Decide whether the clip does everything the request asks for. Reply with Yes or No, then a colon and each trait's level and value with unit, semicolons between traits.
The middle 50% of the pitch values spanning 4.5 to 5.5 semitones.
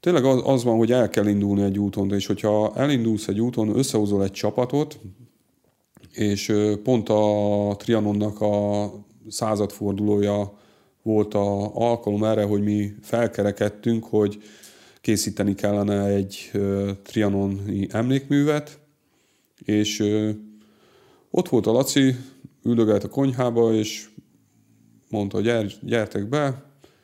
No: narrow, 2.4 semitones